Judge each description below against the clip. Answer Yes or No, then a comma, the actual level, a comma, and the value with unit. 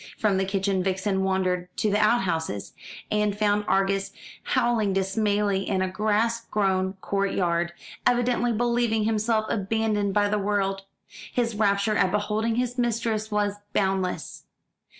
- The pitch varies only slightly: Yes, narrow, 2.3 semitones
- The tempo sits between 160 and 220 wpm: No, average, 140 wpm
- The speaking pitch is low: No, high, 205 Hz